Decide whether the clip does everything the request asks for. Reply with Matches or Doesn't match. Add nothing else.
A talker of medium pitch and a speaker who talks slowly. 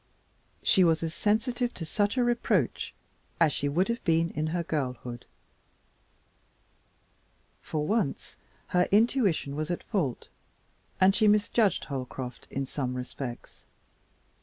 Matches